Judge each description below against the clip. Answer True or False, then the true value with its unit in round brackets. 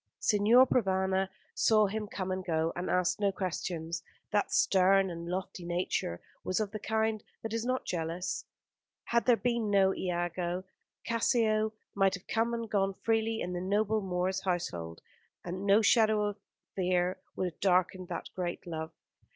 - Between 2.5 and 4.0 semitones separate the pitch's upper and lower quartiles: True (3.3 semitones)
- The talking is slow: False (165 wpm)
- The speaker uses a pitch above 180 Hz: True (190 Hz)